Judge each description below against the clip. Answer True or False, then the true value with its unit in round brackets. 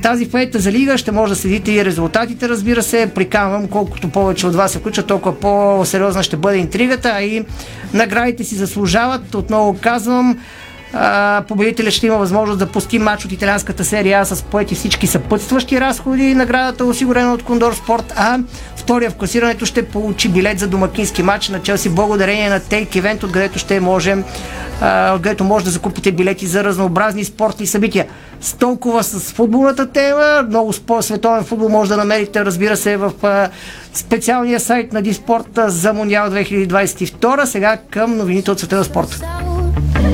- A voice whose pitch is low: False (210 Hz)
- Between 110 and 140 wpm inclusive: False (160 wpm)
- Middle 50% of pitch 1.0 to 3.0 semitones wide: True (2.7 semitones)